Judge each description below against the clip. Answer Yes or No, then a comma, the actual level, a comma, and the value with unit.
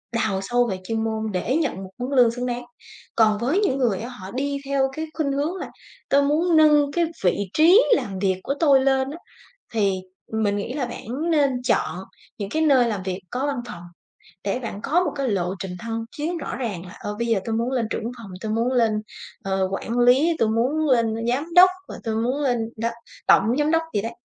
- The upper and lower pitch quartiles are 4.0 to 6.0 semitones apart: Yes, average, 4.5 semitones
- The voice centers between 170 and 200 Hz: No, high, 245 Hz